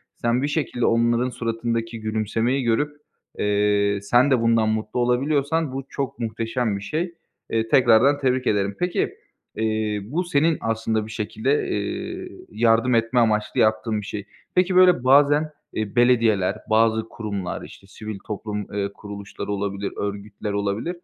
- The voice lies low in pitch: Yes, low, 115 Hz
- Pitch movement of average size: Yes, average, 3.4 semitones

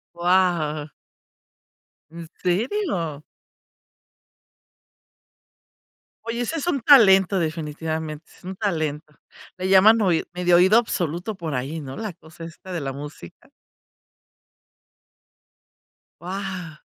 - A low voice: No, medium, 175 Hz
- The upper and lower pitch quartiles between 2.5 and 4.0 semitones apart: Yes, average, 3.7 semitones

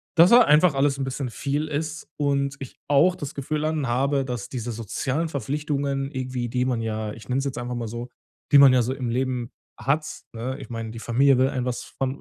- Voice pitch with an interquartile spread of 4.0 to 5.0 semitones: No, average, 2.7 semitones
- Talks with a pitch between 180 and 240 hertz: No, low, 135 Hz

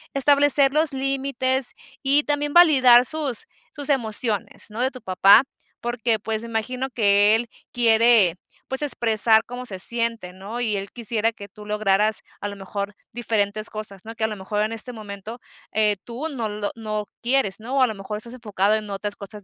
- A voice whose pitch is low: No, high, 225 Hz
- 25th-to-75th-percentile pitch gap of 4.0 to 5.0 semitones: No, average, 3.4 semitones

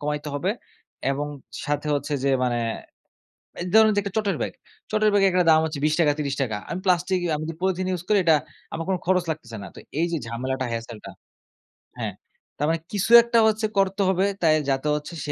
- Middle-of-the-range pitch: Yes, medium, 165 Hz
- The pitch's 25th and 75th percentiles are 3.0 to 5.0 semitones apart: Yes, average, 4.7 semitones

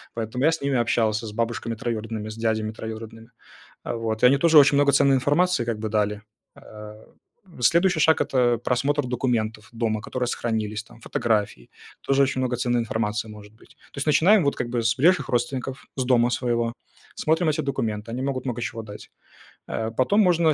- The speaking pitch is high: No, low, 120 Hz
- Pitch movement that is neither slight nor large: Yes, average, 3.8 semitones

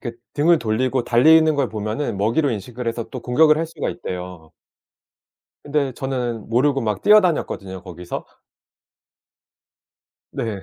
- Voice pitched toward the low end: Yes, low, 125 Hz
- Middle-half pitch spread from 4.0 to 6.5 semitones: Yes, wide, 5.5 semitones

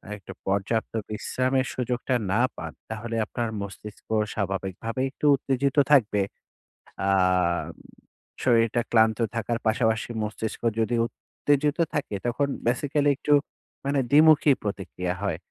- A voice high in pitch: No, low, 115 Hz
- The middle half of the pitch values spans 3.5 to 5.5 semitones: Yes, average, 4.0 semitones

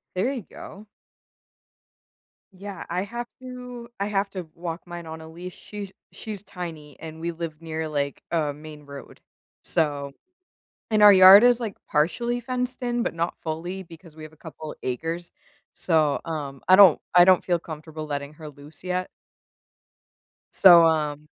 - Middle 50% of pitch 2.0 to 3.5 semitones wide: No, average, 4.1 semitones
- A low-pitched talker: No, medium, 170 Hz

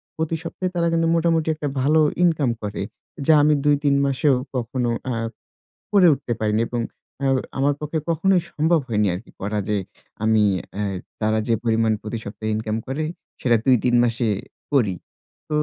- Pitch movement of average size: No, wide, 6.0 semitones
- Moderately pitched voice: No, low, 130 Hz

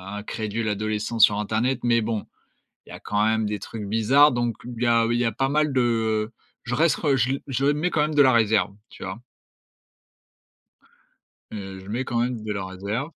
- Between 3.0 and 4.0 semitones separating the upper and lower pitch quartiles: Yes, average, 3.3 semitones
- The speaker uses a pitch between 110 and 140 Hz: Yes, low, 115 Hz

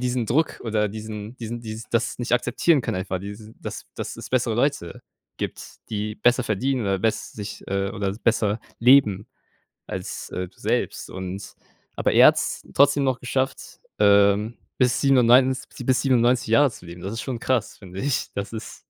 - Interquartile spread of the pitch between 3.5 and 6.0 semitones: Yes, average, 3.9 semitones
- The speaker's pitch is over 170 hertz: No, low, 115 Hz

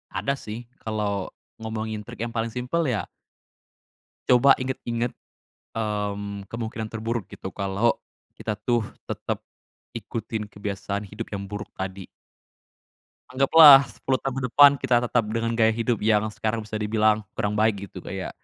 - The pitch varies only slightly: Yes, narrow, 2.3 semitones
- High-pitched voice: No, low, 110 Hz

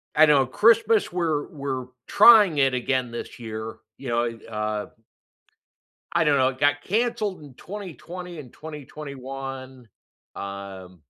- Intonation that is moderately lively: No, wide, 5.8 semitones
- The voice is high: No, low, 135 Hz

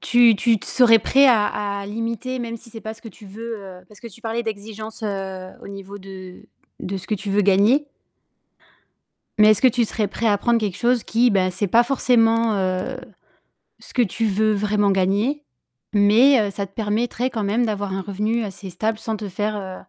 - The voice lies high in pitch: Yes, high, 215 Hz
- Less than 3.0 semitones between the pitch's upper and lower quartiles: Yes, narrow, 2.6 semitones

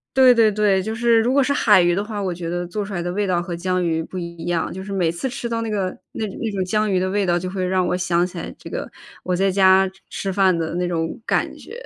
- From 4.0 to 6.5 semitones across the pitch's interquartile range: No, average, 3.1 semitones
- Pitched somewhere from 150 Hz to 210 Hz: Yes, high, 190 Hz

